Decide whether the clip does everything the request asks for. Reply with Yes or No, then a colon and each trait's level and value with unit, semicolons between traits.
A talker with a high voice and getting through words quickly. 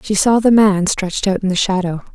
Yes: high, 195 Hz; fast, 250 wpm